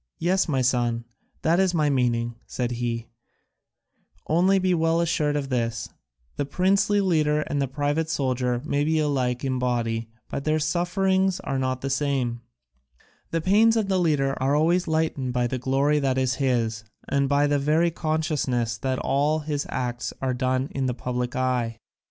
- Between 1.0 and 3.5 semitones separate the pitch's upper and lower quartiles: No, average, 4.1 semitones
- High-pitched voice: No, medium, 140 Hz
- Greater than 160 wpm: Yes, average, 170 wpm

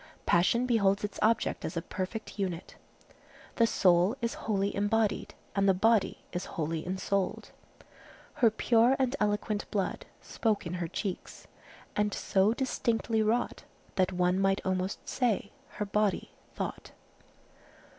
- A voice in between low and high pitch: No, high, 205 Hz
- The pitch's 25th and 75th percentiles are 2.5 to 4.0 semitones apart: Yes, average, 3.1 semitones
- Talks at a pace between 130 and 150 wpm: Yes, slow, 135 wpm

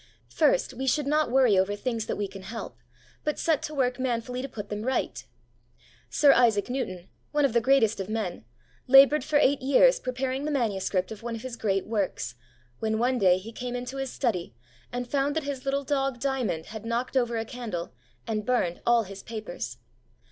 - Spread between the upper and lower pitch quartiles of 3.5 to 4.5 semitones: Yes, average, 4.2 semitones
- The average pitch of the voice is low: No, high, 240 Hz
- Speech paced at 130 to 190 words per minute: No, average, 200 wpm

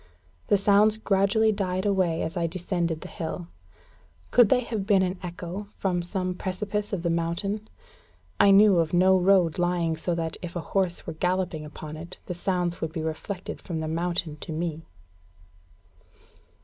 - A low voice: No, medium, 180 Hz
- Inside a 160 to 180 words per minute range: Yes, average, 170 wpm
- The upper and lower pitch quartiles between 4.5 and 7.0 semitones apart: No, average, 2.7 semitones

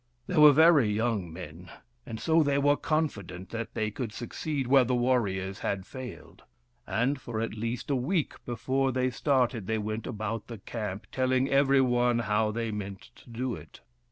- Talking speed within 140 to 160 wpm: No, average, 180 wpm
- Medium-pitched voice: No, low, 120 Hz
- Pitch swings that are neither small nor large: Yes, average, 3.8 semitones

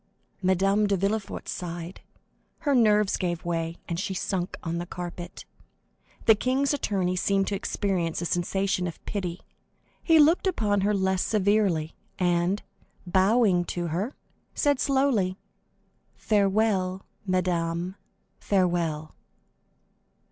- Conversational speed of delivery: No, slow, 115 wpm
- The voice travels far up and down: No, average, 3.1 semitones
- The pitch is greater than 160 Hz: Yes, high, 190 Hz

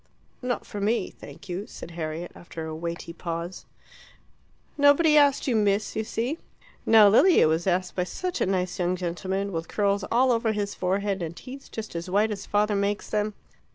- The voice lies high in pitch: Yes, high, 200 Hz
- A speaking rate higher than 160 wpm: Yes, average, 185 wpm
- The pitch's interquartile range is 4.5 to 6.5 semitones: No, average, 4.0 semitones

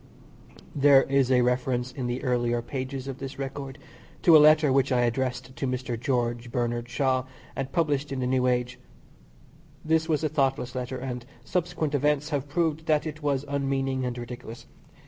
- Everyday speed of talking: Yes, average, 175 wpm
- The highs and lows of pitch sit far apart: No, narrow, 2.6 semitones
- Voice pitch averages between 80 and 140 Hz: Yes, low, 135 Hz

